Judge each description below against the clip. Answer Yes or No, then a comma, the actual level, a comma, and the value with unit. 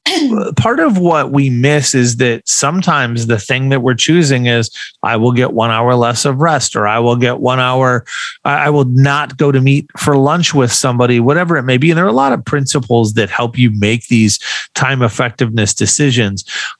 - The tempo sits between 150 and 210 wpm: Yes, fast, 205 wpm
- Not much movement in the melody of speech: No, average, 3.3 semitones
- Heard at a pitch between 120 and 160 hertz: Yes, low, 130 Hz